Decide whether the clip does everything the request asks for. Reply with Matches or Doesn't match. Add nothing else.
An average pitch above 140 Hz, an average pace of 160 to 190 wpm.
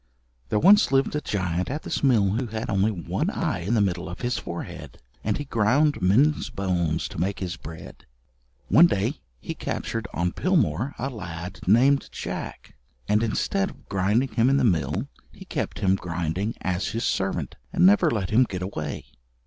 Doesn't match